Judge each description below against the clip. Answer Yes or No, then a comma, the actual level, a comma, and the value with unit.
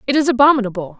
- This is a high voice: Yes, high, 240 Hz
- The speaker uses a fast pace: No, average, 180 wpm